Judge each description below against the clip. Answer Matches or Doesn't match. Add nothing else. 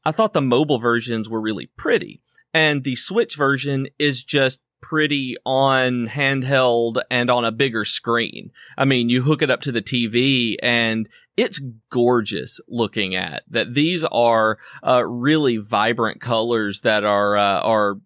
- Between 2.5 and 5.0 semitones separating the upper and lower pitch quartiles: Matches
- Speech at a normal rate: Matches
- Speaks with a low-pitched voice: Matches